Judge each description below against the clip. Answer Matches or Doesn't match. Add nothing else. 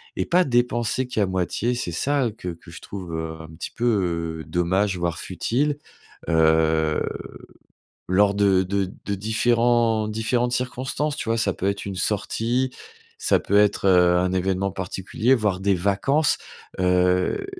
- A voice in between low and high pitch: Doesn't match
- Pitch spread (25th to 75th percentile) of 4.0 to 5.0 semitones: Matches